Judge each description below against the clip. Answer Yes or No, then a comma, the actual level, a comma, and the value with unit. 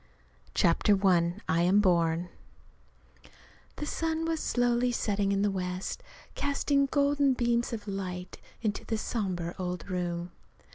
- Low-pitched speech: No, high, 200 Hz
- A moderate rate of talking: No, slow, 130 wpm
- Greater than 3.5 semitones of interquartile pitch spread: Yes, average, 5.3 semitones